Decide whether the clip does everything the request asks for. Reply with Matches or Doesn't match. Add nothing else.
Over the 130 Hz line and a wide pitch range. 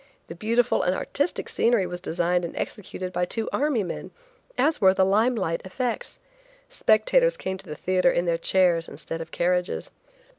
Doesn't match